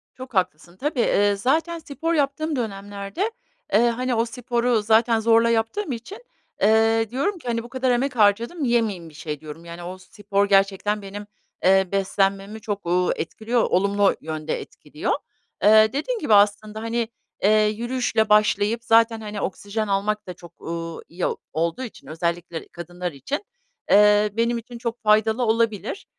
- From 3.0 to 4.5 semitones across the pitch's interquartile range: Yes, average, 3.3 semitones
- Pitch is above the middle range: Yes, high, 215 Hz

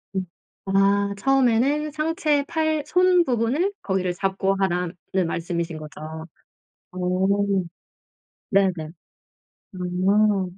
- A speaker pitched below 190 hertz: No, high, 200 Hz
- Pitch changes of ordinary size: No, wide, 7.9 semitones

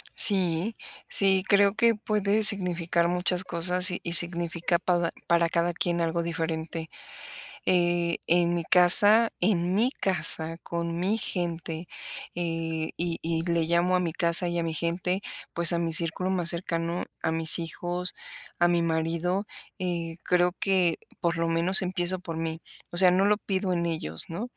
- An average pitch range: No, narrow, 1.6 semitones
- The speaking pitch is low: No, medium, 175 Hz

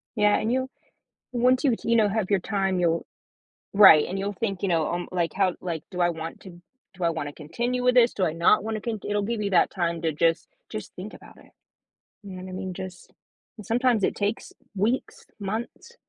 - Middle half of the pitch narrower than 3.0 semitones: No, average, 4.2 semitones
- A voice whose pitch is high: Yes, high, 195 Hz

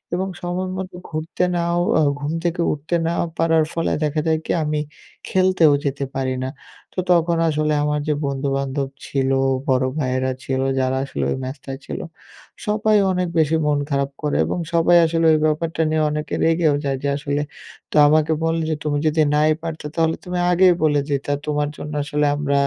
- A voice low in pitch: No, medium, 155 Hz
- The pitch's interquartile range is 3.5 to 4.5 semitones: No, average, 2.7 semitones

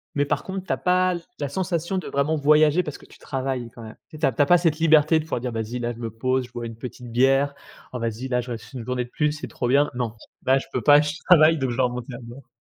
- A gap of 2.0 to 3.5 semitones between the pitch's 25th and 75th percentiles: No, average, 3.9 semitones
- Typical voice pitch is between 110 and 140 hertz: Yes, low, 135 Hz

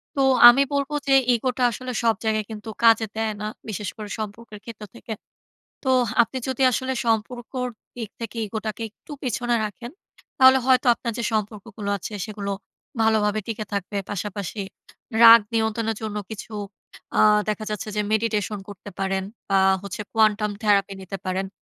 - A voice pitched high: Yes, high, 220 Hz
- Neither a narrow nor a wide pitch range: No, narrow, 2.0 semitones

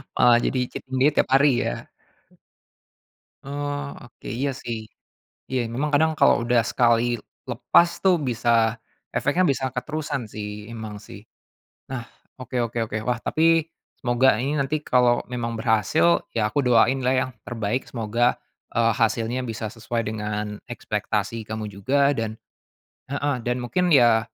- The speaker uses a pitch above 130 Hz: No, low, 120 Hz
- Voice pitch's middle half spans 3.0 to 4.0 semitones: Yes, average, 3.3 semitones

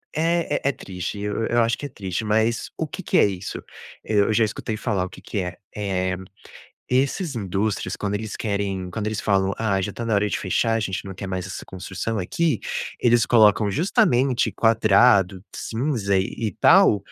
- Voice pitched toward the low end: Yes, low, 105 Hz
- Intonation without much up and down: No, average, 3.3 semitones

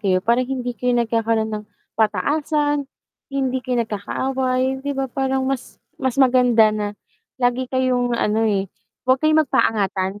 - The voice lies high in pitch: Yes, very high, 250 Hz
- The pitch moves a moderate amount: Yes, average, 3.2 semitones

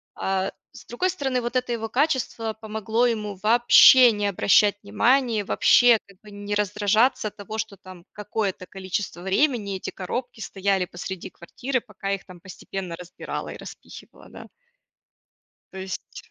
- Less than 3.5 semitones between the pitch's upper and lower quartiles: No, average, 3.8 semitones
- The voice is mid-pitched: No, high, 210 Hz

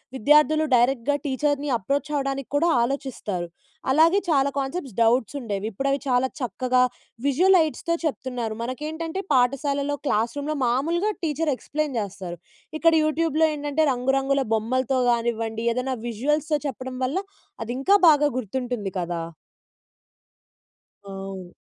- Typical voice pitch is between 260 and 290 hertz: Yes, very high, 270 Hz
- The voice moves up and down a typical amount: Yes, average, 4.1 semitones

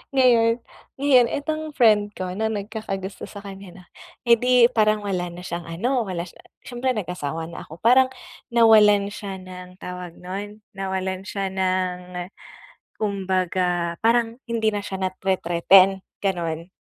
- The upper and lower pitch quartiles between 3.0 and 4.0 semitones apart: Yes, average, 3.6 semitones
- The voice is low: No, high, 195 Hz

